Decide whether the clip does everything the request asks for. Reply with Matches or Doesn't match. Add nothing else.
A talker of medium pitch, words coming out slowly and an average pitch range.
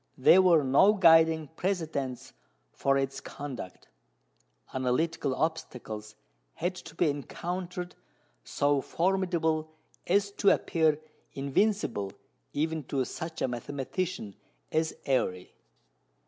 Matches